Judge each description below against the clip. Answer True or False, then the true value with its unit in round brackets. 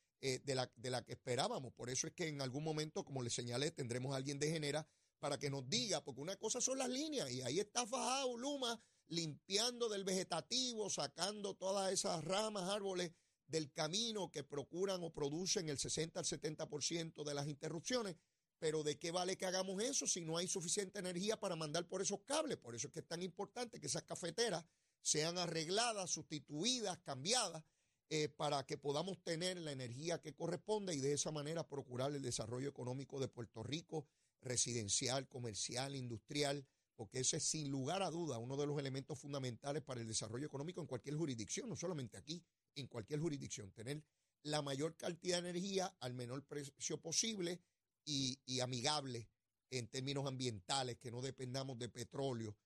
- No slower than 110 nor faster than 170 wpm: False (180 wpm)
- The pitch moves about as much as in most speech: True (5.0 semitones)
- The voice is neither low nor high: True (150 Hz)